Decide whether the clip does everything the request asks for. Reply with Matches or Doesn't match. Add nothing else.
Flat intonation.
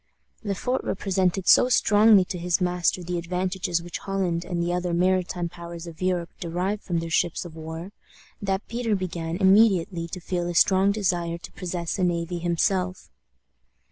Matches